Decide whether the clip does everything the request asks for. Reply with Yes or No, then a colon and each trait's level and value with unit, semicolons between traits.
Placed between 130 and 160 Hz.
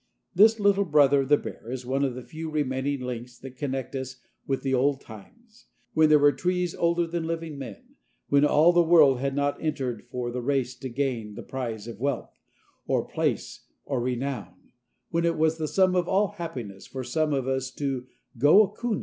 Yes: medium, 140 Hz